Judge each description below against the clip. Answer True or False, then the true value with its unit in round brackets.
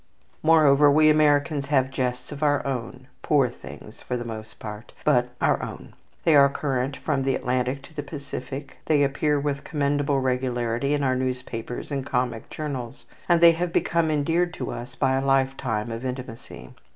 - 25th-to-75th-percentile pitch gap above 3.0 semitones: False (2.6 semitones)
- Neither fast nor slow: True (175 wpm)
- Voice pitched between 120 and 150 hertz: True (135 Hz)